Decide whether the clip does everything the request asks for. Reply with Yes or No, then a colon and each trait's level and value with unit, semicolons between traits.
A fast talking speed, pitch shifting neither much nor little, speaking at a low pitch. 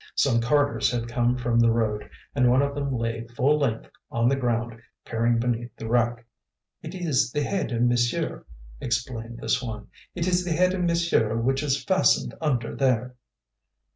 No: average, 175 wpm; average, 3.4 semitones; low, 120 Hz